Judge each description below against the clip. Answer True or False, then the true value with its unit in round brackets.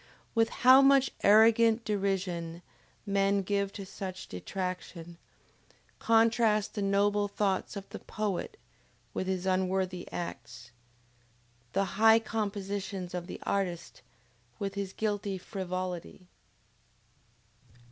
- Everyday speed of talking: False (105 wpm)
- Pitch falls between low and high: False (195 Hz)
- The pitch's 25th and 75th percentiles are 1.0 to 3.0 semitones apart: True (2.4 semitones)